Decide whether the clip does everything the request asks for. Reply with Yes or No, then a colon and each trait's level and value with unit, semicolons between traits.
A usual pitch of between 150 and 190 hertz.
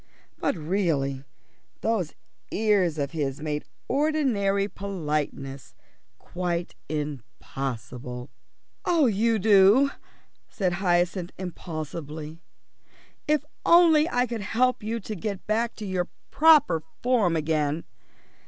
Yes: medium, 185 Hz